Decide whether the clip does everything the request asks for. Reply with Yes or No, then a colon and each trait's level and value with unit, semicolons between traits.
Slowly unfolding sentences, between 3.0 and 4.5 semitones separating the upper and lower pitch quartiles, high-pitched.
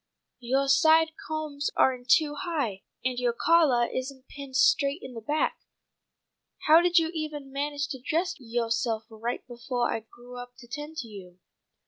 No: average, 165 wpm; average, 4.1 semitones; very high, 265 Hz